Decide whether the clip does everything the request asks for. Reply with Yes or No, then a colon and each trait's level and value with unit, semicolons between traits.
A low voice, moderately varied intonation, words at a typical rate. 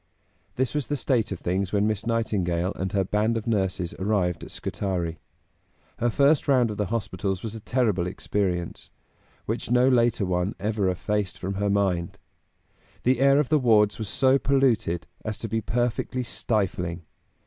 Yes: low, 105 Hz; average, 4.1 semitones; average, 170 wpm